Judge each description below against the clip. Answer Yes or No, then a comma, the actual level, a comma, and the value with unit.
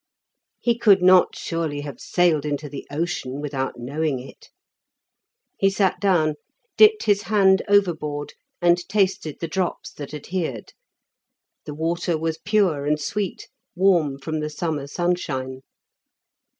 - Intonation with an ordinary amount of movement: Yes, average, 4.4 semitones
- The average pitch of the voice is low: No, medium, 160 Hz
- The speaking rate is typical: No, slow, 130 wpm